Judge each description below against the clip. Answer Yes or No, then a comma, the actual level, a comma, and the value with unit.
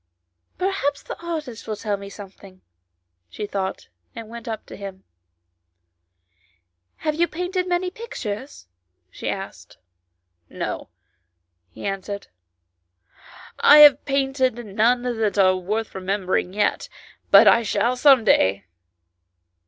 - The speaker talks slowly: Yes, slow, 120 wpm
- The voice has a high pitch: Yes, high, 220 Hz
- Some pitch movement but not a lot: No, wide, 6.1 semitones